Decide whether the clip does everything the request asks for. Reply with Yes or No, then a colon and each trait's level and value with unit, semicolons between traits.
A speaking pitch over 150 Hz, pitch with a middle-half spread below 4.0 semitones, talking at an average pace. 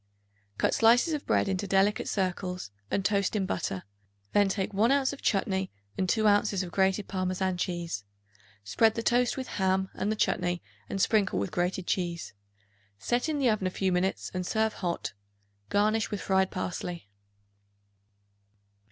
Yes: high, 190 Hz; average, 2.8 semitones; average, 160 wpm